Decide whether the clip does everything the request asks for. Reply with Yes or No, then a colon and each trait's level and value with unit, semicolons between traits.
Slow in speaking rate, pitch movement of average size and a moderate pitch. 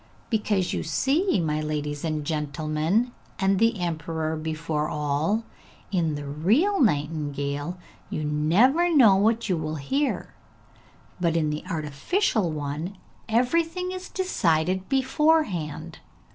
No: slow, 115 wpm; wide, 7.1 semitones; medium, 165 Hz